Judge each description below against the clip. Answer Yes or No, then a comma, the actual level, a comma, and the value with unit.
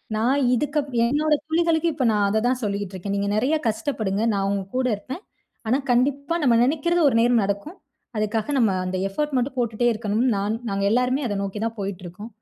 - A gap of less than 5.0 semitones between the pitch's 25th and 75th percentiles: No, wide, 5.6 semitones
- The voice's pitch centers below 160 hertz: No, high, 235 Hz